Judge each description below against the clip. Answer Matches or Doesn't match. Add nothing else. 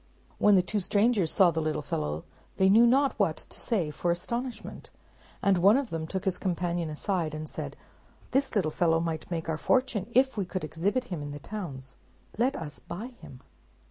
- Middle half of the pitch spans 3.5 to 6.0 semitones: Matches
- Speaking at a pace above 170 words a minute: Matches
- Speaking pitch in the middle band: Matches